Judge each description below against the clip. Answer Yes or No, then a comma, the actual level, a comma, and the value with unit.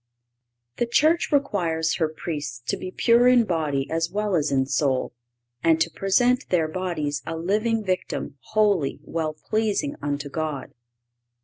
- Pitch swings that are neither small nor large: No, wide, 6.0 semitones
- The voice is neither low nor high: Yes, medium, 165 Hz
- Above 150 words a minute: No, average, 145 wpm